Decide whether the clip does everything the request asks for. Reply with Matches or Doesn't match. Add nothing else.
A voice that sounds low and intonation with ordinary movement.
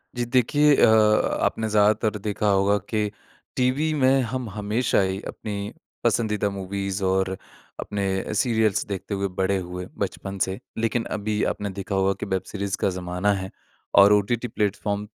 Doesn't match